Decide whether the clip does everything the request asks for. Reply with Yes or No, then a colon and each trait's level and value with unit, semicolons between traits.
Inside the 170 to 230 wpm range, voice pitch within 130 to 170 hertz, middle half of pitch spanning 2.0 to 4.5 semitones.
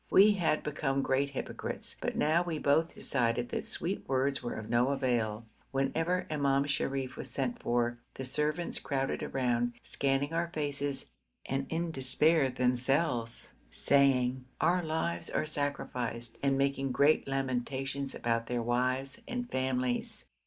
No: average, 140 wpm; low, 135 Hz; average, 3.0 semitones